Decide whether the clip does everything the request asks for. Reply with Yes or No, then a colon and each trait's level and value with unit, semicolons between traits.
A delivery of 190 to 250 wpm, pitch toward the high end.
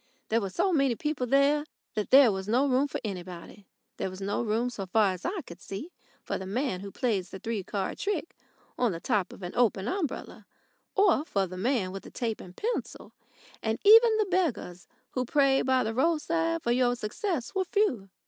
Yes: fast, 205 wpm; high, 240 Hz